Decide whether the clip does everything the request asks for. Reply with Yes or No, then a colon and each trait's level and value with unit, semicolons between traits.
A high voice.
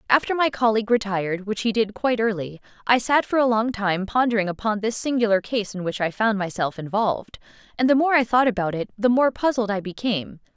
Yes: high, 220 Hz